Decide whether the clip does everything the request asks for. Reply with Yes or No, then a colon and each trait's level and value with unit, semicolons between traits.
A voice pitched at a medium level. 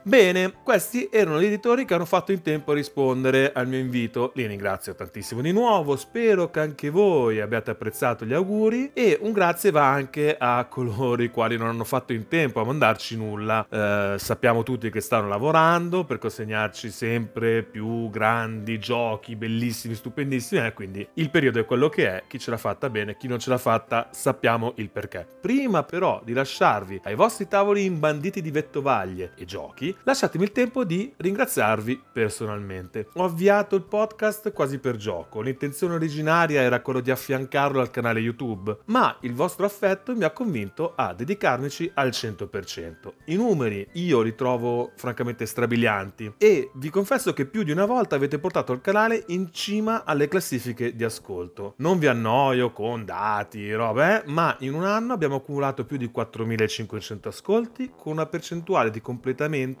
No: low, 130 Hz